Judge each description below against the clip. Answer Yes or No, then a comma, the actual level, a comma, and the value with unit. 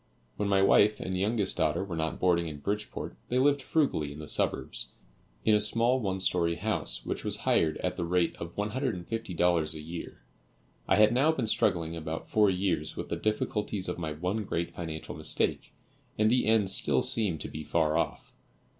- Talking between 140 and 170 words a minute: No, average, 190 wpm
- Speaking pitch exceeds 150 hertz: No, very low, 95 Hz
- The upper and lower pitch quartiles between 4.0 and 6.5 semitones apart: Yes, average, 4.6 semitones